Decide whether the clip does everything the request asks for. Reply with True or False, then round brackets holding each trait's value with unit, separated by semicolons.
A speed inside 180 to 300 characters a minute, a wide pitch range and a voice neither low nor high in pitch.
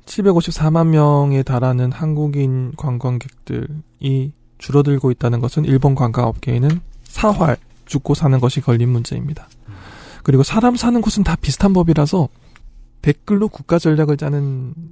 False (295 characters per minute; 4.1 semitones; 145 Hz)